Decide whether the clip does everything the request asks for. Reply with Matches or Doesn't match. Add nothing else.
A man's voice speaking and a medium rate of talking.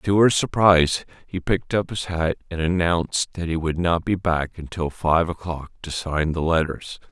Matches